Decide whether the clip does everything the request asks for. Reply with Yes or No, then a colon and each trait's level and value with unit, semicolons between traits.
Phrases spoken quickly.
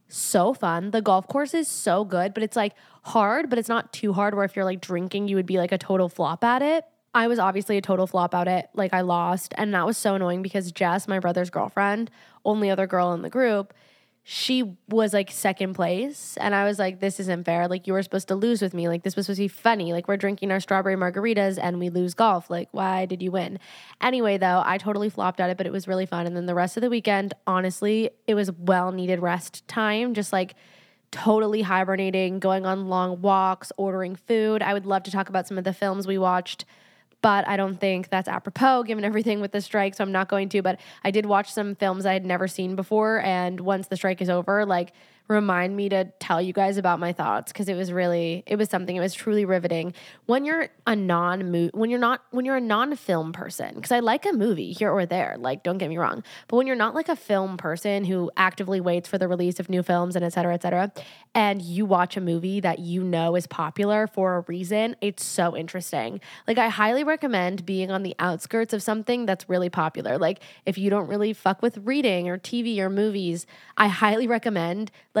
Yes: fast, 235 wpm